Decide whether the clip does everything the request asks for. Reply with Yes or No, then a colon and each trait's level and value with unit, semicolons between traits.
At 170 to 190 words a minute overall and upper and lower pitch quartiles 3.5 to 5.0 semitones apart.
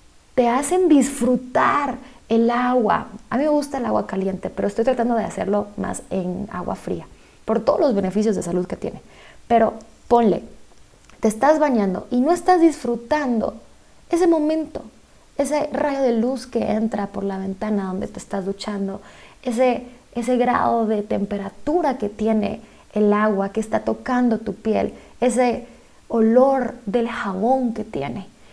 No: average, 155 wpm; average, 3.9 semitones